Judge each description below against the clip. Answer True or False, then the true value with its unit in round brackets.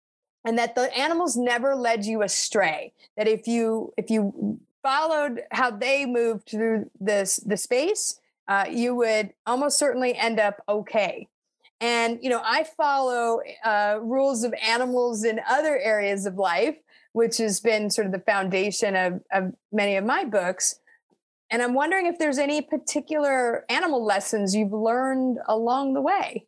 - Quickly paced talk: False (160 wpm)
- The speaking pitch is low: False (230 Hz)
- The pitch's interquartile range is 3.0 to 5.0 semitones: True (4.1 semitones)